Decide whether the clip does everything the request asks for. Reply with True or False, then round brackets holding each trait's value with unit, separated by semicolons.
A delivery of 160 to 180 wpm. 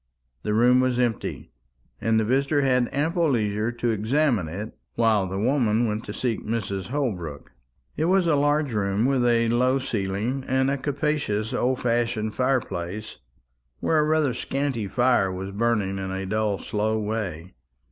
True (165 wpm)